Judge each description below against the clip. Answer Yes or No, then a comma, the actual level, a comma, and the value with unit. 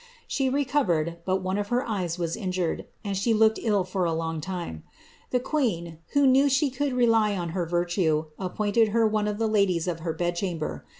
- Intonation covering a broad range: No, average, 4.9 semitones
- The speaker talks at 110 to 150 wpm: No, average, 175 wpm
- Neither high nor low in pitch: No, high, 195 Hz